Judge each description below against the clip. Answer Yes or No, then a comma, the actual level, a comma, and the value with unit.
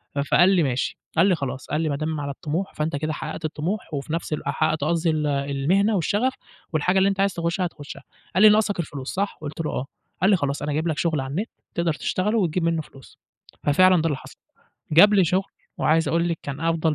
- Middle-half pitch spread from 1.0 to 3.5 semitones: No, average, 3.9 semitones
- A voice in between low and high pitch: Yes, medium, 165 Hz